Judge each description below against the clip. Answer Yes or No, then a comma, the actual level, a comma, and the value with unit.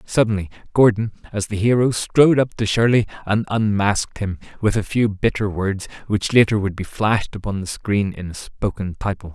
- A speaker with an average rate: Yes, average, 185 wpm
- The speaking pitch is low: Yes, low, 105 Hz